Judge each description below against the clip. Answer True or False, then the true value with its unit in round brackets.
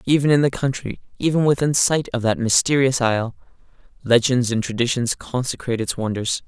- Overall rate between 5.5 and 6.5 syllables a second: True (5.7 syllables/s)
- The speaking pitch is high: False (125 Hz)